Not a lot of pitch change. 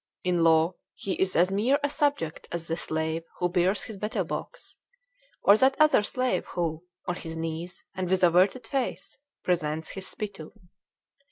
No: average, 4.1 semitones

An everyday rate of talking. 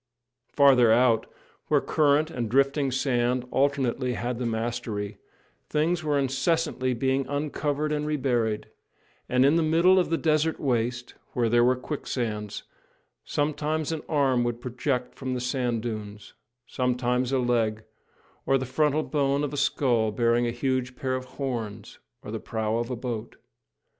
Yes: average, 155 wpm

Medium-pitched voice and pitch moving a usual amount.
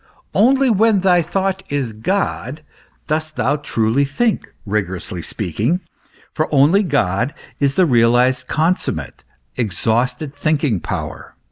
No: medium, 145 Hz; wide, 7.3 semitones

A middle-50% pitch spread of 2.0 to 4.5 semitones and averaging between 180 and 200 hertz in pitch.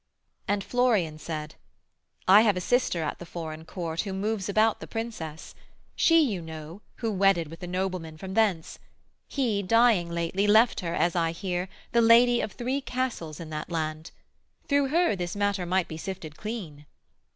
No: average, 5.2 semitones; high, 190 Hz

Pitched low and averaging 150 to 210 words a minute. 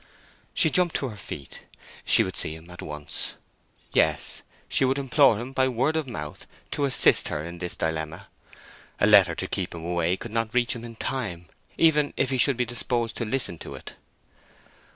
Yes: low, 115 Hz; average, 195 wpm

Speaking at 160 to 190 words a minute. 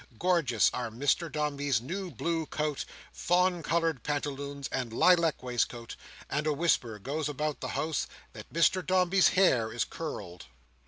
No: average, 145 wpm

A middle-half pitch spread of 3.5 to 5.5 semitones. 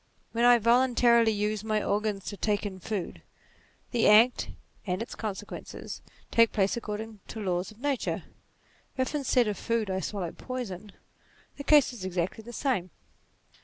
No: average, 3.0 semitones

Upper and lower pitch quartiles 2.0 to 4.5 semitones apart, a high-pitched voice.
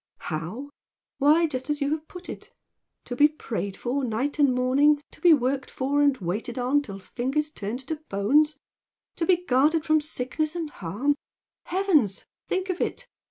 Yes: average, 3.8 semitones; very high, 285 Hz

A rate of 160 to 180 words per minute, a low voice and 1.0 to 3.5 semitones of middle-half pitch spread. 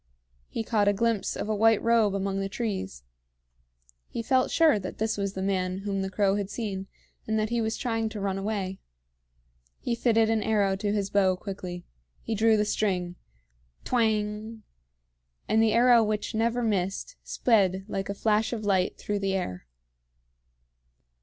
No: average, 170 wpm; high, 210 Hz; narrow, 2.4 semitones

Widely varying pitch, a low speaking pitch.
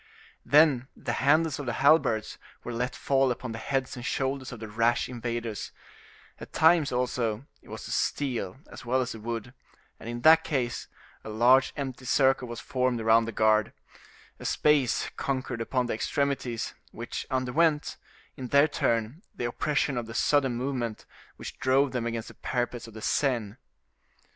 No: average, 2.8 semitones; low, 125 Hz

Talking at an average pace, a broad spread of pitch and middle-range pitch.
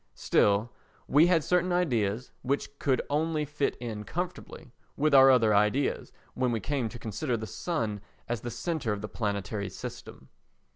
No: average, 160 wpm; wide, 5.8 semitones; low, 125 Hz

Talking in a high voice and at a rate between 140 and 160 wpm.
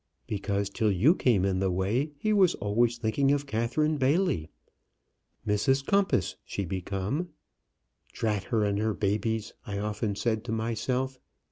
No: low, 110 Hz; average, 145 wpm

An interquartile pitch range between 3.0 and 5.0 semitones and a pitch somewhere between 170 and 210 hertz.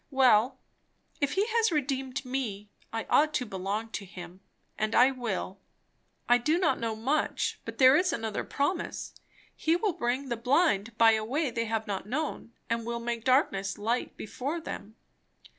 No: average, 4.4 semitones; high, 240 Hz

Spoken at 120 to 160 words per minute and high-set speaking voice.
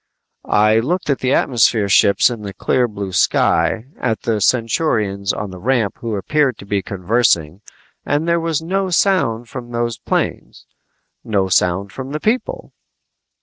No: average, 155 wpm; low, 115 Hz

